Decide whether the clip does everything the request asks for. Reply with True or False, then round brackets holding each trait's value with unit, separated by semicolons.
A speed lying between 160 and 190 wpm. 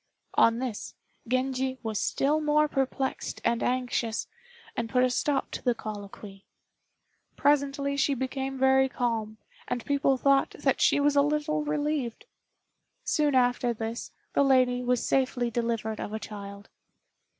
False (140 wpm)